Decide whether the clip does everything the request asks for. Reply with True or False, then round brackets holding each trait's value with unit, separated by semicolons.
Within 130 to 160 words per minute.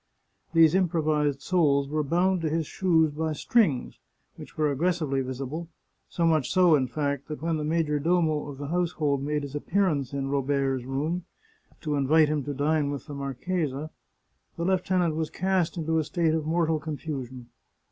False (175 wpm)